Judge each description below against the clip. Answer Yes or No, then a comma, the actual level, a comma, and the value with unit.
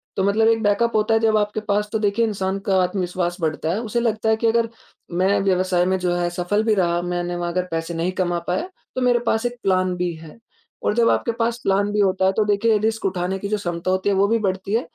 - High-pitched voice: Yes, high, 195 Hz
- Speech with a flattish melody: No, average, 3.6 semitones